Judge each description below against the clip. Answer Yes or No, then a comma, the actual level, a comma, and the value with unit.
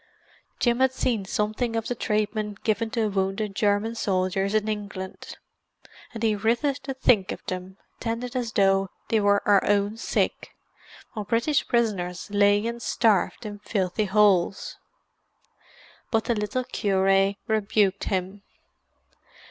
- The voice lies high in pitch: Yes, high, 210 Hz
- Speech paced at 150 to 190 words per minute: No, slow, 135 wpm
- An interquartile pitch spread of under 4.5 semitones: Yes, average, 2.7 semitones